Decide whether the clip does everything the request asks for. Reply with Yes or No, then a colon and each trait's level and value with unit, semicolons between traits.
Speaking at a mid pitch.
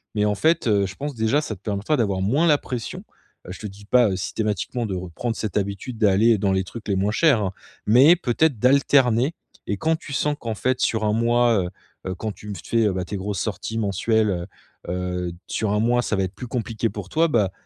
No: low, 110 Hz